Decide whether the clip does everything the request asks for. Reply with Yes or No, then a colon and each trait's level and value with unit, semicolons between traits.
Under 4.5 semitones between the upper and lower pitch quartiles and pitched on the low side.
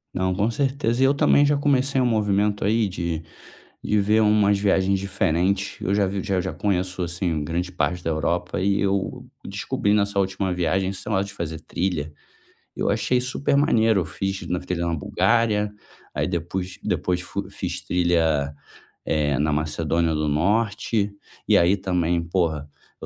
Yes: average, 3.4 semitones; very low, 95 Hz